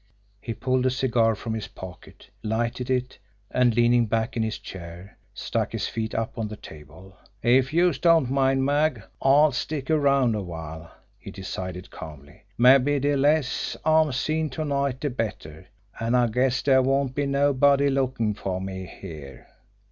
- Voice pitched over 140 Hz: No, low, 125 Hz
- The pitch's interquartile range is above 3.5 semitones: Yes, average, 4.8 semitones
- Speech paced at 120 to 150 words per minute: No, average, 165 wpm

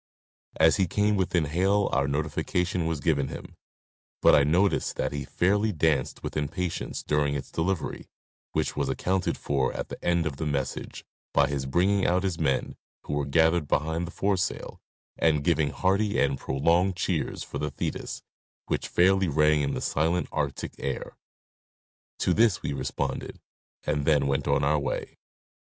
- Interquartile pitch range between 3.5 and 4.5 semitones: Yes, average, 4.1 semitones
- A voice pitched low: Yes, very low, 80 Hz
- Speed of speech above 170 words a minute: No, average, 165 wpm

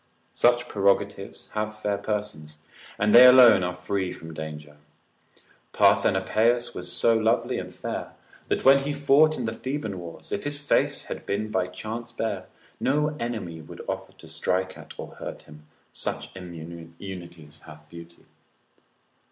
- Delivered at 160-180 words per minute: No, average, 150 wpm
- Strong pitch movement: Yes, wide, 5.7 semitones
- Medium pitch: No, low, 100 Hz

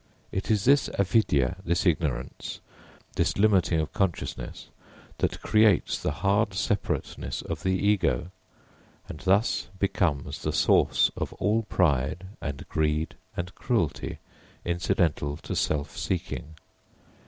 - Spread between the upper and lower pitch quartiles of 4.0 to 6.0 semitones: Yes, average, 4.6 semitones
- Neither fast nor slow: No, slow, 120 wpm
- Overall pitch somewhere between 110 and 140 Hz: No, very low, 90 Hz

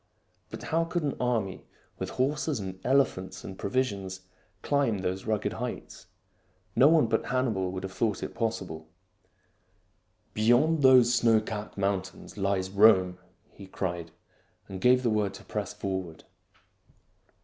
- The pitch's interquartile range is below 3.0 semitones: No, average, 4.9 semitones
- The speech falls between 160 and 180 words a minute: No, average, 150 wpm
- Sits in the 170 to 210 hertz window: No, low, 105 Hz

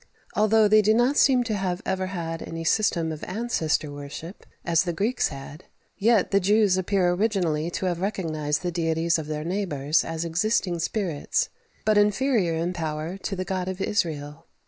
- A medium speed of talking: Yes, average, 175 wpm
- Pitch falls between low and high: Yes, medium, 180 Hz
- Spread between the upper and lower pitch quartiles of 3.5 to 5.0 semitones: Yes, average, 4.2 semitones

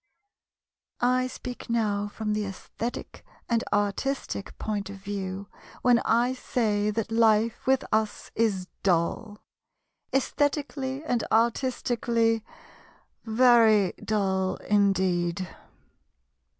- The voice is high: Yes, high, 220 Hz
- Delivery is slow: Yes, slow, 95 wpm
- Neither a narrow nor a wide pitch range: Yes, average, 3.1 semitones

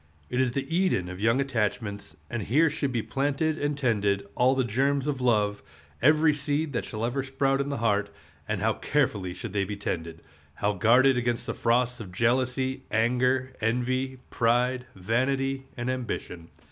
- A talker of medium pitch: No, low, 125 Hz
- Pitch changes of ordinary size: Yes, average, 3.8 semitones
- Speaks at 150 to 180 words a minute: Yes, average, 170 wpm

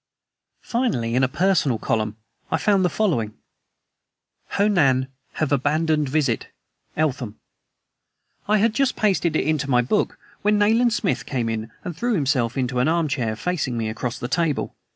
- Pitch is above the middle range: No, medium, 150 Hz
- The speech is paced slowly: No, average, 160 wpm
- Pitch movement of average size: No, wide, 7.4 semitones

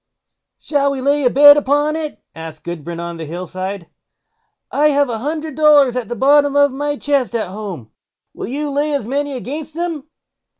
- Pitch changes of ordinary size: No, wide, 5.8 semitones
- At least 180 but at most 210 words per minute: Yes, average, 185 wpm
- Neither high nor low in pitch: No, very high, 280 Hz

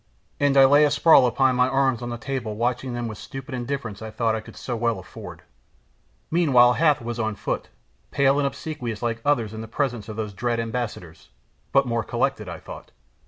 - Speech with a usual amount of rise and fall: Yes, average, 3.3 semitones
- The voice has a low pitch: Yes, low, 120 Hz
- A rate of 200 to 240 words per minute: Yes, fast, 205 wpm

